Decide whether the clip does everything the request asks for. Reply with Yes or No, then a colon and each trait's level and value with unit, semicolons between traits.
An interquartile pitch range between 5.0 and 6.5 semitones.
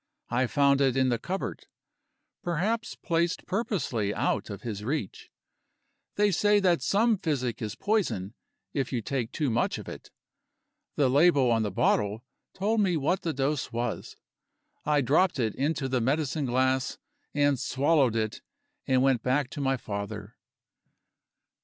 Yes: wide, 5.6 semitones